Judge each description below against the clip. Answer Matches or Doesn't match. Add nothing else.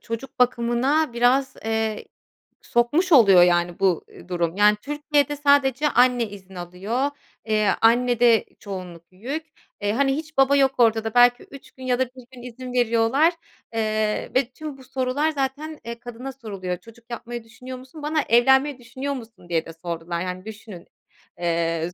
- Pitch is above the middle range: Matches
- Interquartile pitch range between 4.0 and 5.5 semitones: Matches